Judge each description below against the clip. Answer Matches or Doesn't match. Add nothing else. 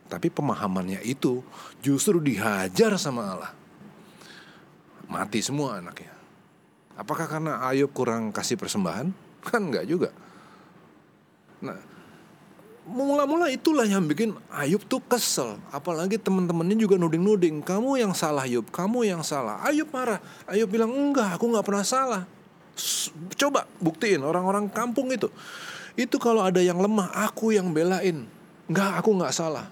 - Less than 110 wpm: Doesn't match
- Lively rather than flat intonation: Matches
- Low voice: Doesn't match